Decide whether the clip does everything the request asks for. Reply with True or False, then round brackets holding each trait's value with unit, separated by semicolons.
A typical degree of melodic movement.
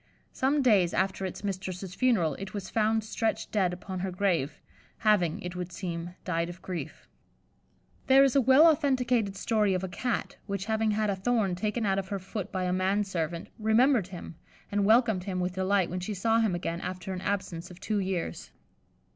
True (3.3 semitones)